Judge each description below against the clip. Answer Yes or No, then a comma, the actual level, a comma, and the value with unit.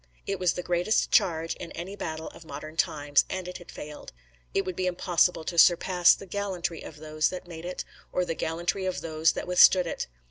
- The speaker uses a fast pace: Yes, fast, 210 wpm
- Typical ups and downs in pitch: No, narrow, 2.2 semitones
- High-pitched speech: No, medium, 175 Hz